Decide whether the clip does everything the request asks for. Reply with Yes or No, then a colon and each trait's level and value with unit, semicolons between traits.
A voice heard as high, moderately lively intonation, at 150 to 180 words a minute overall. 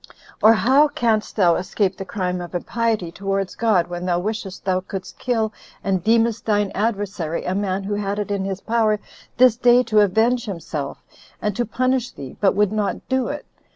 No: high, 205 Hz; average, 3.5 semitones; average, 190 wpm